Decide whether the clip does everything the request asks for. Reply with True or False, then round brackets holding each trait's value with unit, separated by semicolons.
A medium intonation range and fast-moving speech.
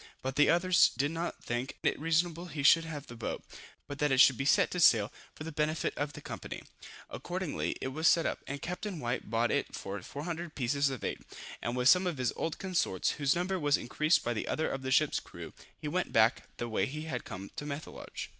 True (4.2 semitones; 225 wpm)